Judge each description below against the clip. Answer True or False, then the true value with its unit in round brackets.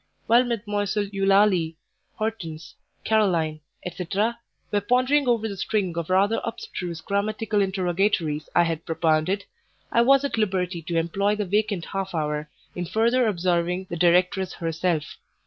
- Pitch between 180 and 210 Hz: True (190 Hz)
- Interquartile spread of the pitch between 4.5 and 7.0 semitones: False (3.8 semitones)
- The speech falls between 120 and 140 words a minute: True (135 wpm)